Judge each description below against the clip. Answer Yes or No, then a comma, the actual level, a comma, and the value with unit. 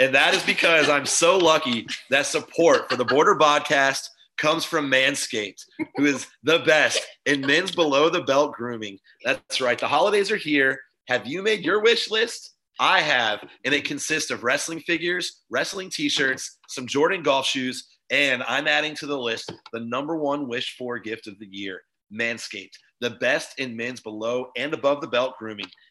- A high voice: No, medium, 140 Hz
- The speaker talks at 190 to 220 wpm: No, average, 180 wpm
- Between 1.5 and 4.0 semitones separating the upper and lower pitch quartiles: No, average, 4.9 semitones